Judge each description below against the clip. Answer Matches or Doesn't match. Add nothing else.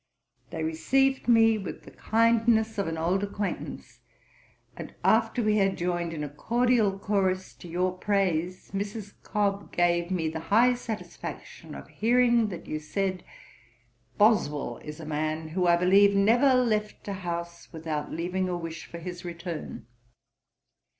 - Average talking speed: Matches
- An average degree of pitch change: Matches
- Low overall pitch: Doesn't match